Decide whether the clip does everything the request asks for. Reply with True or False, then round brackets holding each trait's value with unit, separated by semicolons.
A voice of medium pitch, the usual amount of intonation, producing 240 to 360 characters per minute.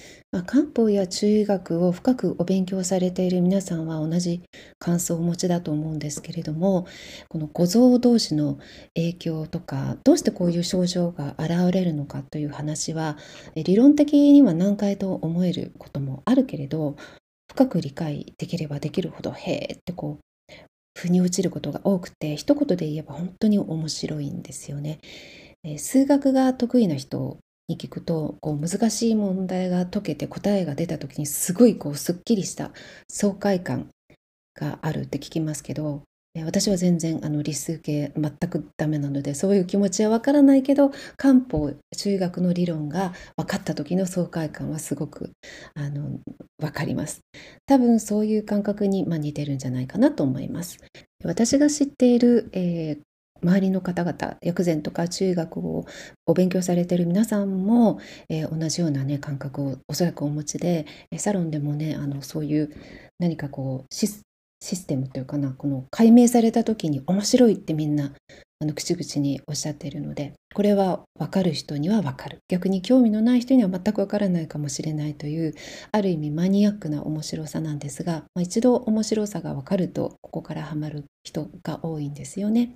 True (170 Hz; 4.8 semitones; 340 characters per minute)